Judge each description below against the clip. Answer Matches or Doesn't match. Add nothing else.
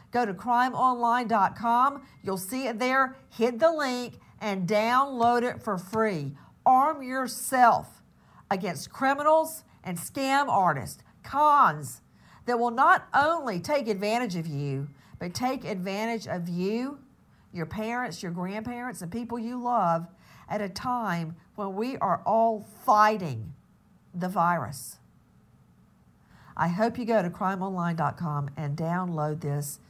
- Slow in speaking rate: Matches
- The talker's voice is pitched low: Doesn't match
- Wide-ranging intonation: Matches